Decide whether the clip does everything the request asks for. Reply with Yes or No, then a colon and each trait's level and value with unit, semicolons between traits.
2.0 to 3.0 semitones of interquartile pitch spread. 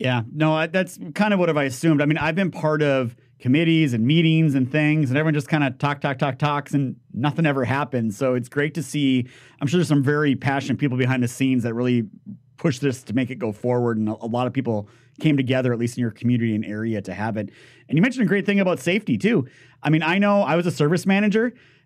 No: average, 4.2 semitones